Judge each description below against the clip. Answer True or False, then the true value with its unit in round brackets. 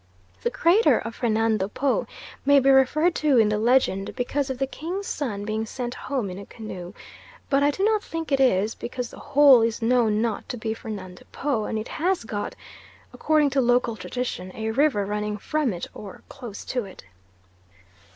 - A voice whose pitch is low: False (245 Hz)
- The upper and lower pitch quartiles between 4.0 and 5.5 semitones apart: True (4.7 semitones)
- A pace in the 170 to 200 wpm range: True (190 wpm)